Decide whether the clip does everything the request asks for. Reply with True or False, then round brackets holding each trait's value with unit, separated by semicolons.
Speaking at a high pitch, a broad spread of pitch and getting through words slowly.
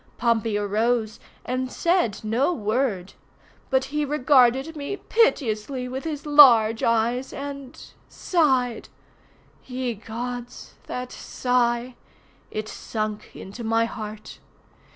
False (245 Hz; 3.4 semitones; 95 wpm)